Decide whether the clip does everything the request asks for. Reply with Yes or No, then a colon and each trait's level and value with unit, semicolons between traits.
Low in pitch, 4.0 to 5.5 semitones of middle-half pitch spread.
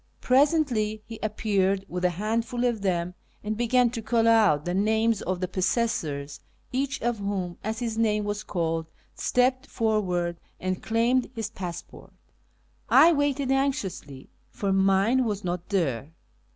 No: high, 215 Hz; average, 4.3 semitones